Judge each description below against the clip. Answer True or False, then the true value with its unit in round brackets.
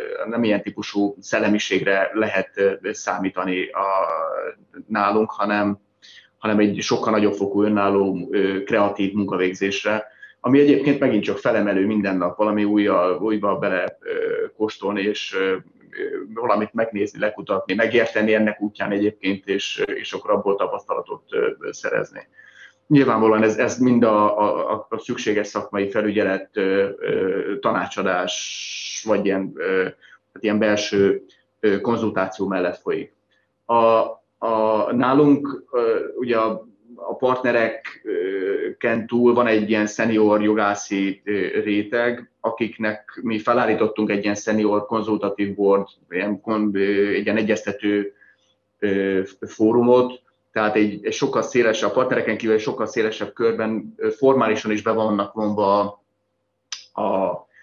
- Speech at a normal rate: True (115 wpm)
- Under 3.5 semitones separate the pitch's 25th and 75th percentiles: True (3.1 semitones)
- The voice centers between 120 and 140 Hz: False (105 Hz)